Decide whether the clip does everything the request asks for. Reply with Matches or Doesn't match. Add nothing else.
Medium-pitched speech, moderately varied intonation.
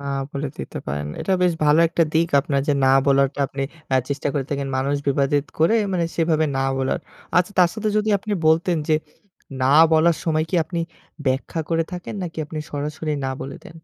Matches